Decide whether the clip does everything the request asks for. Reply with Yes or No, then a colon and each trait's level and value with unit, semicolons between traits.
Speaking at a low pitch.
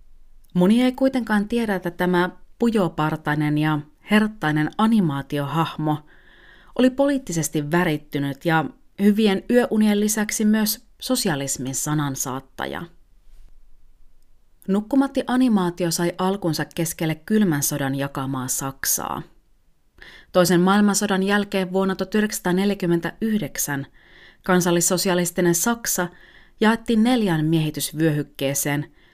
No: medium, 175 Hz